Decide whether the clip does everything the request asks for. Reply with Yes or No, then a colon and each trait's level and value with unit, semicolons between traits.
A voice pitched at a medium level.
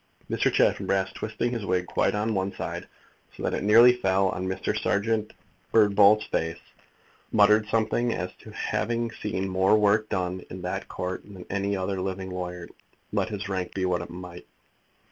No: very low, 95 Hz